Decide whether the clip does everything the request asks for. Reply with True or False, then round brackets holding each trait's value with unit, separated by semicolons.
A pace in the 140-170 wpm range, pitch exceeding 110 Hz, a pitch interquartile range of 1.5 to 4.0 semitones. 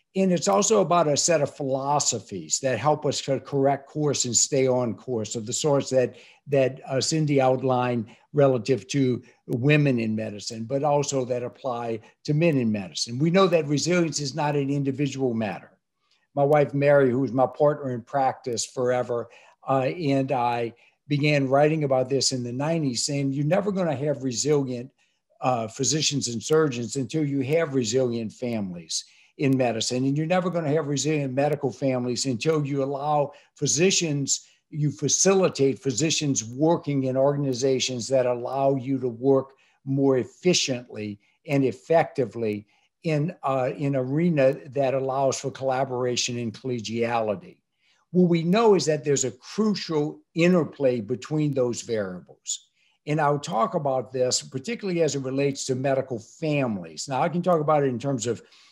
True (160 wpm; 135 Hz; 3.0 semitones)